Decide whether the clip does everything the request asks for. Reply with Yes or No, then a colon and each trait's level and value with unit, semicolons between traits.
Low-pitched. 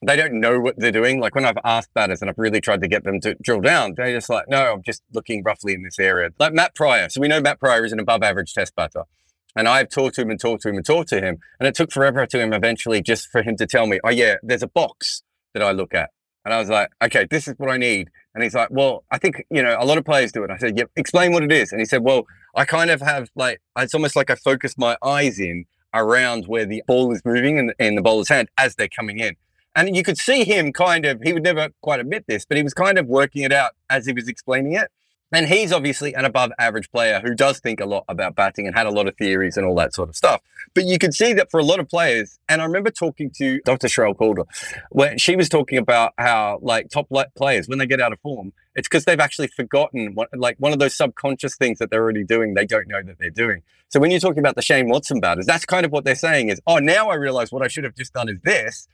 Yes: low, 130 Hz